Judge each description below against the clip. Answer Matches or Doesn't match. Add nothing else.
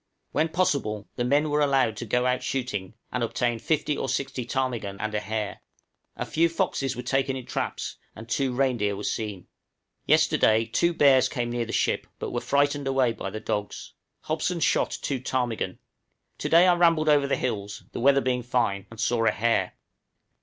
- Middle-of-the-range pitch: Doesn't match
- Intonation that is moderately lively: Matches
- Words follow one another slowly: Doesn't match